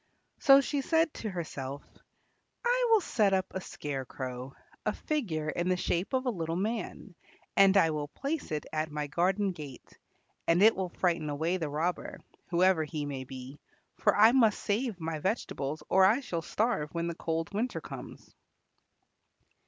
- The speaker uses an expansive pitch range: Yes, wide, 5.8 semitones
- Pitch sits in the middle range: Yes, medium, 175 Hz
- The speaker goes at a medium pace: Yes, average, 170 wpm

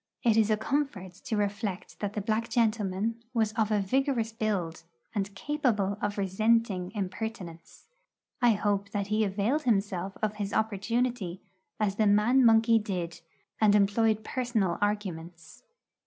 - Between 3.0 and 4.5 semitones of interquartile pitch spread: No, narrow, 2.4 semitones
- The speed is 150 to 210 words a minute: No, average, 140 wpm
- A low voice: No, high, 210 Hz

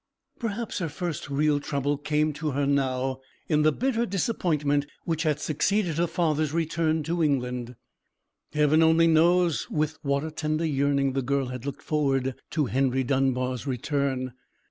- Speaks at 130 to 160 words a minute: Yes, average, 155 wpm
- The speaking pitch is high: No, medium, 150 Hz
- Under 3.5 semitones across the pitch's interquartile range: Yes, average, 2.9 semitones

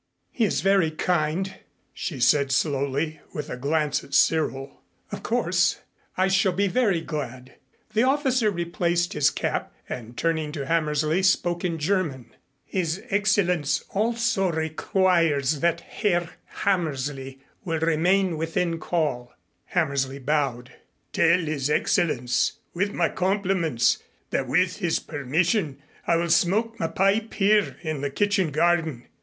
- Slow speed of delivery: Yes, slow, 130 wpm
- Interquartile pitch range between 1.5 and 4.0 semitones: No, average, 4.5 semitones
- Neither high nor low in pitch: Yes, medium, 165 Hz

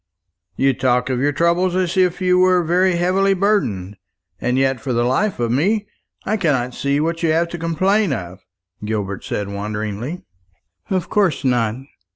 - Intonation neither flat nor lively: No, wide, 7.1 semitones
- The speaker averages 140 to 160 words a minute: No, average, 170 wpm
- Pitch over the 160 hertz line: No, medium, 155 Hz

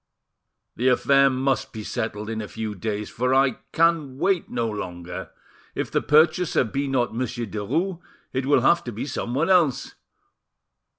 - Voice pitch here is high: No, low, 130 Hz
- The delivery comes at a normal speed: Yes, average, 160 wpm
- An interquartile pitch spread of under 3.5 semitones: No, average, 5.1 semitones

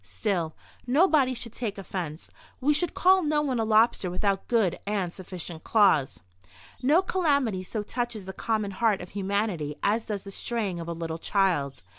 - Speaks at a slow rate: No, average, 170 wpm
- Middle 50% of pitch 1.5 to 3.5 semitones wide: No, average, 5.0 semitones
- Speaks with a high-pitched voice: Yes, high, 205 Hz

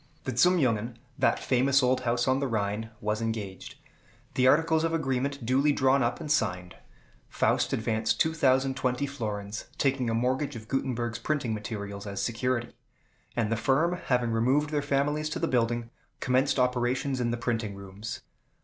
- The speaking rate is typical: Yes, average, 160 wpm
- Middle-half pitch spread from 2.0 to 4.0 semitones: Yes, average, 3.4 semitones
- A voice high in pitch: No, low, 125 Hz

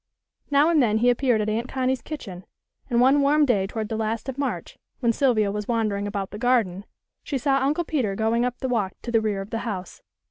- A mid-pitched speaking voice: No, high, 235 Hz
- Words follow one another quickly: Yes, fast, 225 wpm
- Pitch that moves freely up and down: No, average, 4.0 semitones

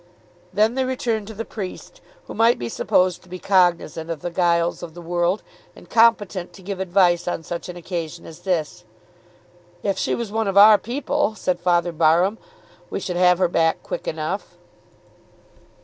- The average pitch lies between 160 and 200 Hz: Yes, medium, 185 Hz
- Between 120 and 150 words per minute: No, average, 180 wpm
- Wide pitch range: No, average, 3.6 semitones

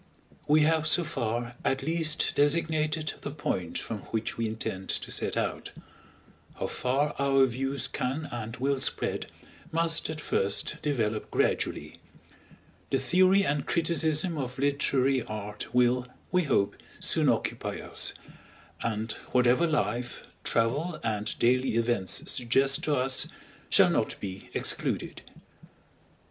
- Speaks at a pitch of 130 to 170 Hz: Yes, low, 135 Hz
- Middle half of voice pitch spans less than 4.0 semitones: No, average, 4.7 semitones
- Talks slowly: Yes, slow, 130 wpm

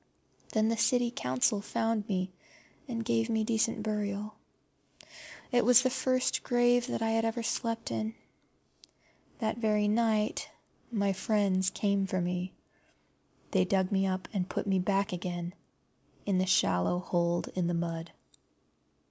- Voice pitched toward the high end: Yes, high, 210 Hz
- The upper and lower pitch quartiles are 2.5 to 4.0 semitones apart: Yes, average, 3.4 semitones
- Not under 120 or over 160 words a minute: Yes, average, 145 wpm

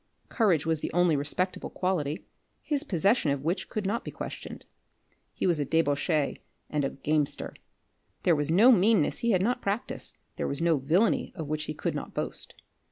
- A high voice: No, medium, 165 Hz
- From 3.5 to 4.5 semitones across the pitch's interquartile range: No, average, 5.0 semitones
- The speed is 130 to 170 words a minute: No, average, 180 wpm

